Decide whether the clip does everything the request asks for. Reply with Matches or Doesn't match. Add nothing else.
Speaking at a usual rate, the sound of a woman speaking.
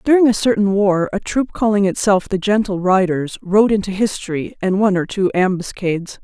Matches